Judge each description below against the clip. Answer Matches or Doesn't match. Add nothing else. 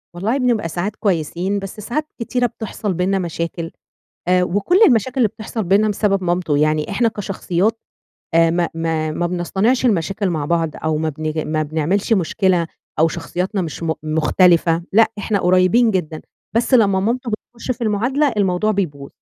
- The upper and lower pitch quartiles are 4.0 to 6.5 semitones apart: Matches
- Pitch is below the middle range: Doesn't match